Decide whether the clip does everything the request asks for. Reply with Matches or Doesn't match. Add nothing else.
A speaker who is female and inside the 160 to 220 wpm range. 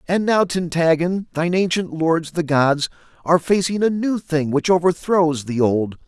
Doesn't match